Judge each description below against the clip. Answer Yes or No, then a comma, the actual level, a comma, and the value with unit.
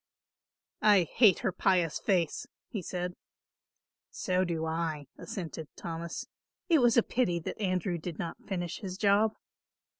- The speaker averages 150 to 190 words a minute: No, average, 140 wpm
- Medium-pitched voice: Yes, medium, 180 Hz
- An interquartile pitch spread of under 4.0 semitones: Yes, average, 3.2 semitones